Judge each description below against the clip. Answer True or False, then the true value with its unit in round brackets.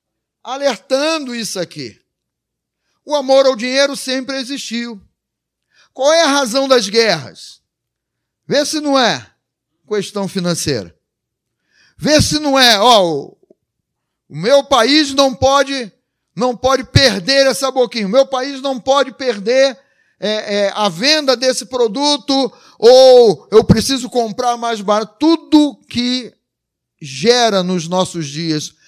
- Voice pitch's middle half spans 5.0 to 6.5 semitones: False (4.4 semitones)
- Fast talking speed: False (125 wpm)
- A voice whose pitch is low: False (255 Hz)